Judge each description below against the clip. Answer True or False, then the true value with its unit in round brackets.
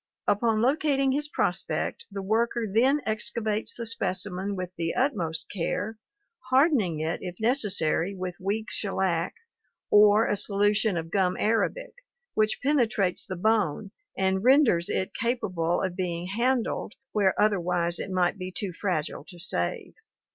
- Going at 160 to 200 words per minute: False (140 wpm)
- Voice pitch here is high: True (205 Hz)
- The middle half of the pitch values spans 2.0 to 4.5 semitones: True (3.9 semitones)